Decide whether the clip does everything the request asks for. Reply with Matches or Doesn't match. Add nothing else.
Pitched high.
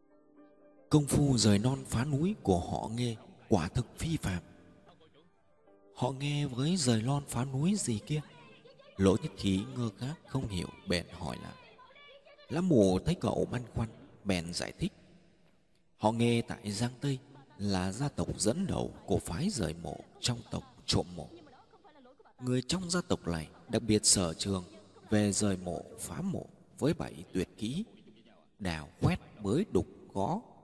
Doesn't match